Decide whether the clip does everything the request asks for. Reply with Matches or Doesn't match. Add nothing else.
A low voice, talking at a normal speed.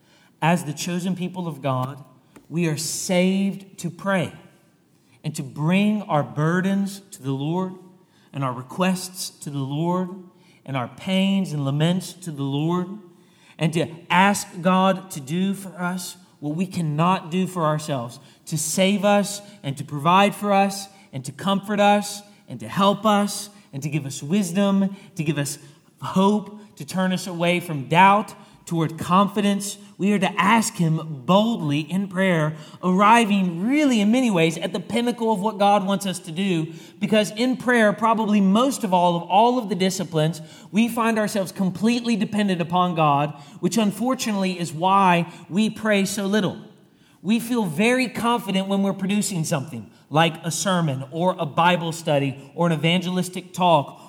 Doesn't match